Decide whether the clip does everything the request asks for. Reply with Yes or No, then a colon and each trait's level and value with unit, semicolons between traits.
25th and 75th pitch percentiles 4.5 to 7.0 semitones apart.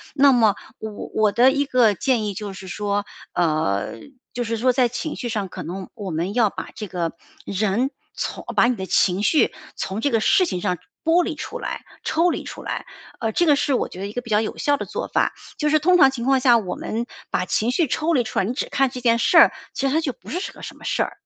Yes: average, 5.2 semitones